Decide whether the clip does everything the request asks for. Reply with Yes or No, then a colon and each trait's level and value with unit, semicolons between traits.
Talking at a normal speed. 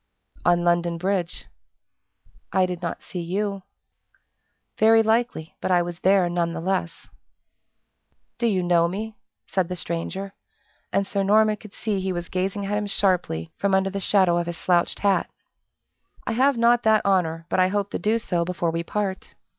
Yes: average, 175 wpm